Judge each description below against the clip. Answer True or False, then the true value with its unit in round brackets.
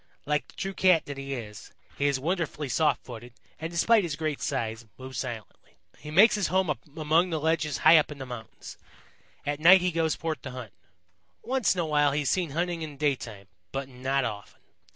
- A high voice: False (150 Hz)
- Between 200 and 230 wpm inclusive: True (205 wpm)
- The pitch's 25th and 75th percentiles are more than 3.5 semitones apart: True (4.0 semitones)